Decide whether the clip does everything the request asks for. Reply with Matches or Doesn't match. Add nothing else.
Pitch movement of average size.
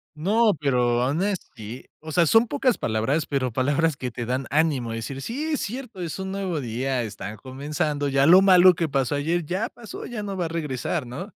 Doesn't match